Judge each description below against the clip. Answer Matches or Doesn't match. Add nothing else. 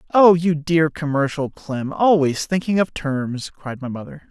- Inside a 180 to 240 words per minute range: Doesn't match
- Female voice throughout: Doesn't match